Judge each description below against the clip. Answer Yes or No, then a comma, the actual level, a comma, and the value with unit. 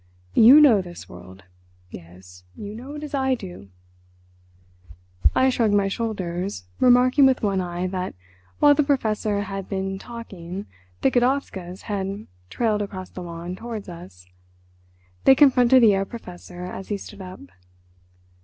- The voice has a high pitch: Yes, high, 200 Hz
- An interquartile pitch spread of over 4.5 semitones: Yes, average, 5.1 semitones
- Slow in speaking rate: No, average, 145 wpm